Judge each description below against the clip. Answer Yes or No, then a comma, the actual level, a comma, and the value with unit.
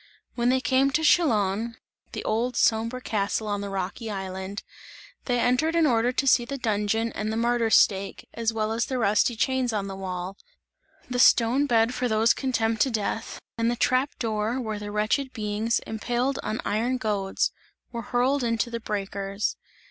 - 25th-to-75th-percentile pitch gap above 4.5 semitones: No, average, 3.0 semitones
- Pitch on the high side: Yes, high, 225 Hz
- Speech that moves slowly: No, average, 180 wpm